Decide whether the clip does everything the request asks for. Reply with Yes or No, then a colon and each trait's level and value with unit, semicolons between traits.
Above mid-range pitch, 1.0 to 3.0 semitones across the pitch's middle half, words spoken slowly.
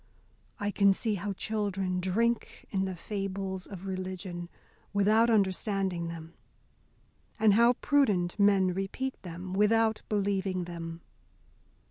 Yes: high, 195 Hz; narrow, 2.4 semitones; slow, 115 wpm